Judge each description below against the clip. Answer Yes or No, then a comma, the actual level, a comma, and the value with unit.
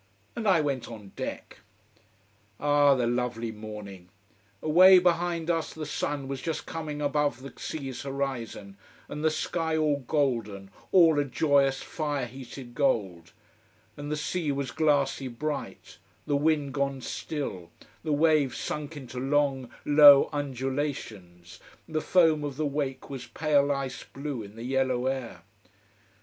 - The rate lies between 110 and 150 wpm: Yes, average, 140 wpm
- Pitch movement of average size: Yes, average, 3.2 semitones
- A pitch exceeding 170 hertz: No, medium, 140 Hz